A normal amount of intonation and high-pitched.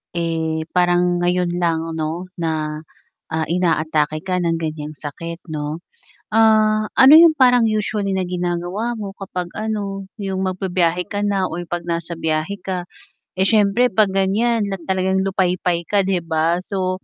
No: average, 3.0 semitones; medium, 180 Hz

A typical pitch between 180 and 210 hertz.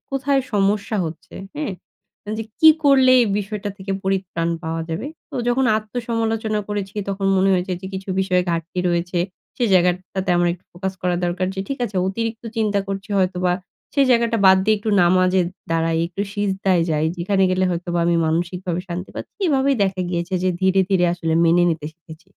Yes: high, 190 Hz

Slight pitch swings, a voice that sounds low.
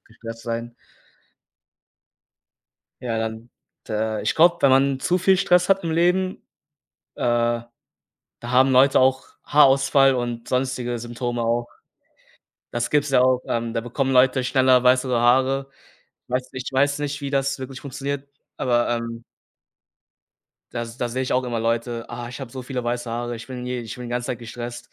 Yes: narrow, 2.3 semitones; low, 125 Hz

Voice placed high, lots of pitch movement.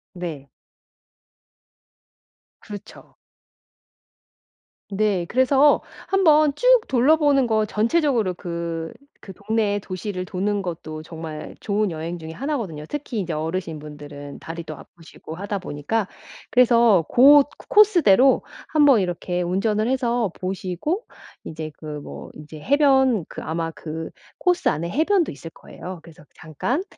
Yes: high, 195 Hz; wide, 8.1 semitones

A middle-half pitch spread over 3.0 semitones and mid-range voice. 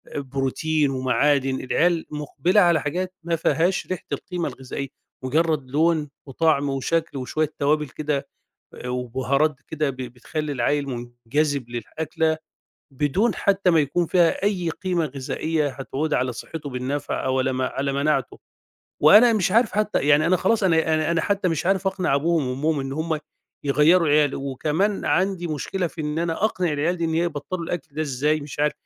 Yes: average, 3.7 semitones; medium, 150 Hz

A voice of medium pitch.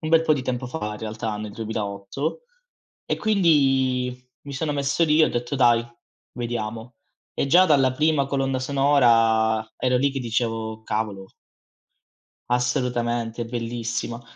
No: low, 125 Hz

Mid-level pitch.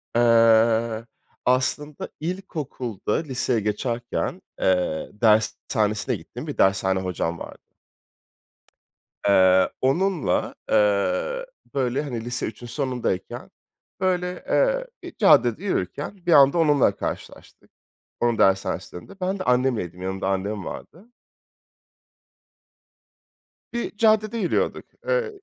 No: low, 125 Hz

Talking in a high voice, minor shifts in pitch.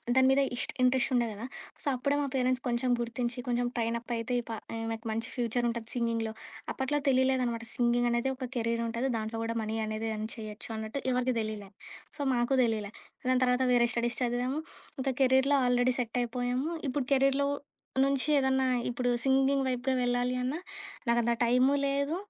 Yes: high, 245 Hz; narrow, 2.1 semitones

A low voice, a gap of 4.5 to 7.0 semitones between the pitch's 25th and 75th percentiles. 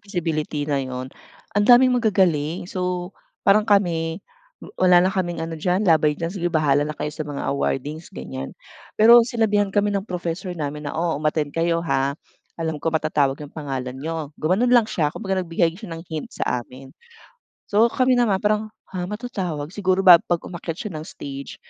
No: medium, 170 Hz; average, 4.8 semitones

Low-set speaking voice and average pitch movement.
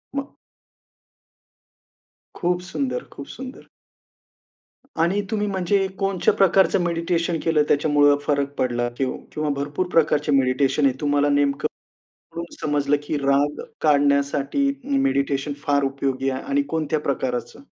No: medium, 145 Hz; average, 3.5 semitones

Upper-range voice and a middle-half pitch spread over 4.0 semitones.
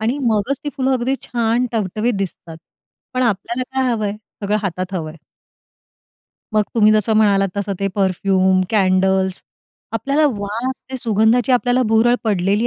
No: high, 215 Hz; average, 3.7 semitones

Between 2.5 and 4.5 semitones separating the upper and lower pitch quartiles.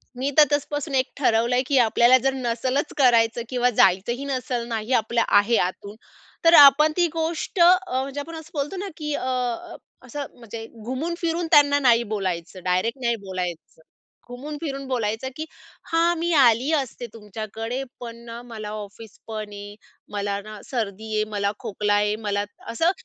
No: average, 5.0 semitones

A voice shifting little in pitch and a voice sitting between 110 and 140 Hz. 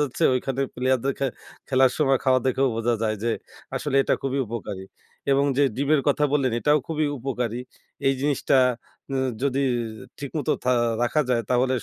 Yes: narrow, 2.0 semitones; low, 135 Hz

